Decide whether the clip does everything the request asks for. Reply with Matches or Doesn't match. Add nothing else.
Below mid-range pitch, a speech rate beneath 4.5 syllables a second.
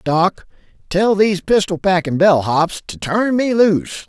Doesn't match